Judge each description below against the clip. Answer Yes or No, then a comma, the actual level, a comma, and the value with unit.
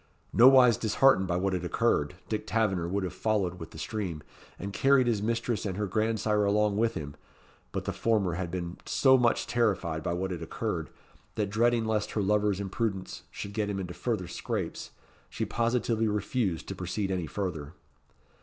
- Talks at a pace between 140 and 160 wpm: No, average, 180 wpm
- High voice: No, low, 100 Hz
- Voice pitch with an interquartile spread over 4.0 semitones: No, average, 3.6 semitones